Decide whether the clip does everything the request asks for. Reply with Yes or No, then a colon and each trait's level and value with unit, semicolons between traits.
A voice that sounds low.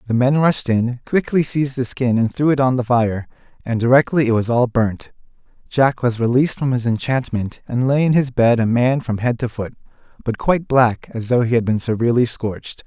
Yes: low, 125 Hz